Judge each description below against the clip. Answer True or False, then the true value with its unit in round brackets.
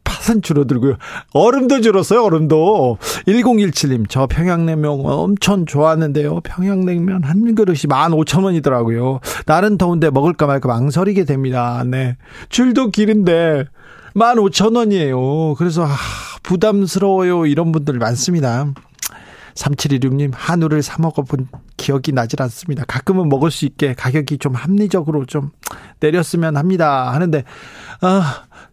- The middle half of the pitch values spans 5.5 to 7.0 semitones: False (5.1 semitones)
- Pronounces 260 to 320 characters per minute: True (280 characters per minute)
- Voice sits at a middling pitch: True (155 Hz)